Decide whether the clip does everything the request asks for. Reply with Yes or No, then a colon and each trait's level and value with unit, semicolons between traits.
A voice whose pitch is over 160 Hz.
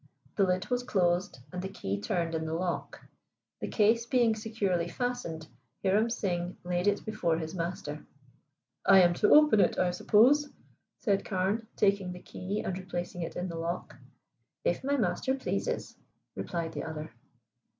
Yes: medium, 185 Hz